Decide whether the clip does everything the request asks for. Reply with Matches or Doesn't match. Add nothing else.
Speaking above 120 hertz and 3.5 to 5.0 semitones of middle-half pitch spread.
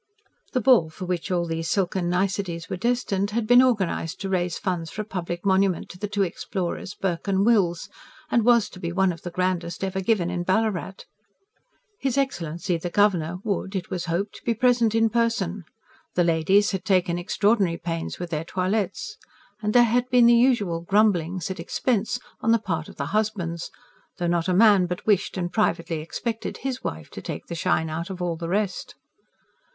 Matches